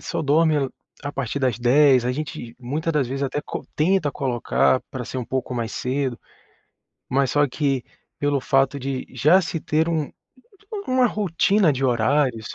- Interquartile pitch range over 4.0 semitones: No, average, 3.1 semitones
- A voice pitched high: No, medium, 140 Hz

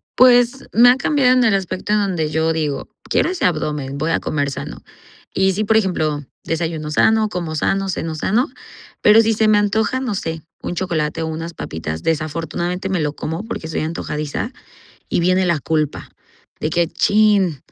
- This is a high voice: No, medium, 170 Hz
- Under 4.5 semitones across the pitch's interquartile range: No, average, 5.2 semitones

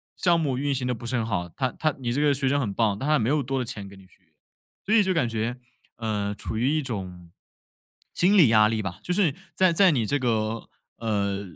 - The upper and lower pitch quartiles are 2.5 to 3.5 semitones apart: No, average, 5.2 semitones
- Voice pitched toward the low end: Yes, low, 120 Hz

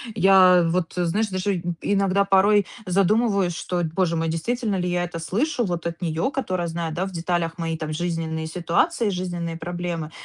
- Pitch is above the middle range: No, medium, 175 Hz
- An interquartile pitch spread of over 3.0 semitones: No, average, 2.7 semitones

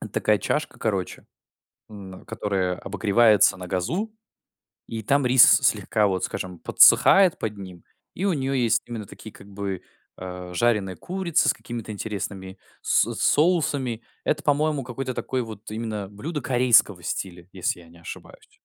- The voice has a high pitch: No, low, 110 Hz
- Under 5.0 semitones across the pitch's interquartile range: No, wide, 5.7 semitones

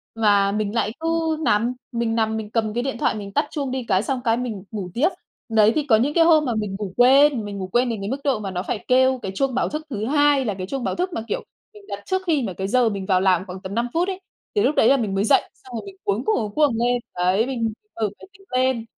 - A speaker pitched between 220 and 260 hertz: Yes, high, 235 Hz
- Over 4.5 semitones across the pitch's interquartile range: Yes, average, 5.0 semitones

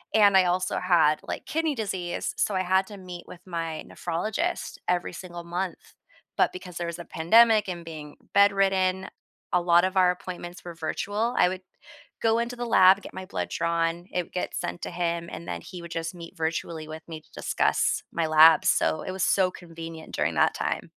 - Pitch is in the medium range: Yes, medium, 180 Hz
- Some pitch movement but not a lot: No, narrow, 2.2 semitones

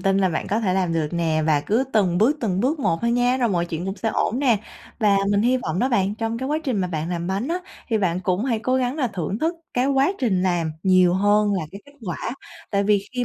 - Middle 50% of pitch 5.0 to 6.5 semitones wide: Yes, average, 5.3 semitones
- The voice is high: Yes, high, 205 Hz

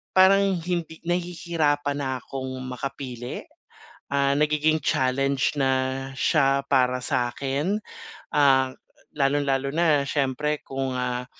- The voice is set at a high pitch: No, medium, 140 Hz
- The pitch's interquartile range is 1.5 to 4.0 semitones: Yes, narrow, 2.6 semitones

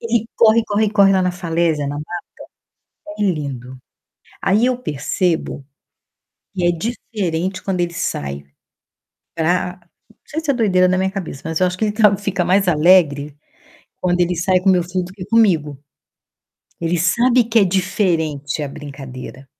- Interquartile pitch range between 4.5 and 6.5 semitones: No, average, 3.9 semitones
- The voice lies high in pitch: No, medium, 180 Hz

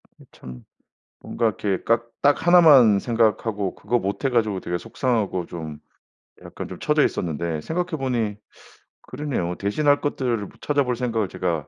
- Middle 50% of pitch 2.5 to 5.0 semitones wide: No, wide, 5.6 semitones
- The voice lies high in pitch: No, low, 115 Hz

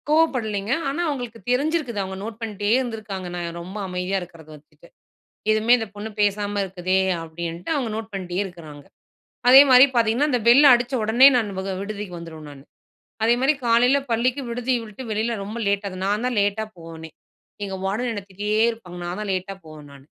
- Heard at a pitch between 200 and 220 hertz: Yes, high, 210 Hz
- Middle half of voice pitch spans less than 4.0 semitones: No, average, 4.3 semitones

